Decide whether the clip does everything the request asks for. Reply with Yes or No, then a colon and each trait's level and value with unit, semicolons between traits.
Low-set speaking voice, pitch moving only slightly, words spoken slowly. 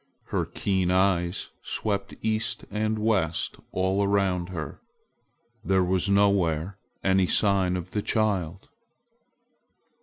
Yes: very low, 95 Hz; narrow, 2.0 semitones; slow, 115 wpm